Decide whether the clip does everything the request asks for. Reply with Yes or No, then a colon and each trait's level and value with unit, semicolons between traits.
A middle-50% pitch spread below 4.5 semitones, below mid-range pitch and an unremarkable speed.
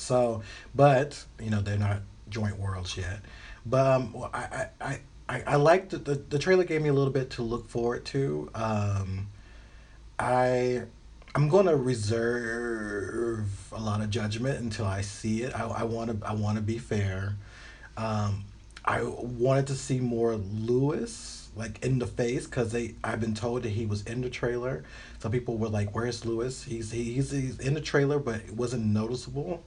Yes: average, 2.9 semitones; low, 115 Hz; average, 175 wpm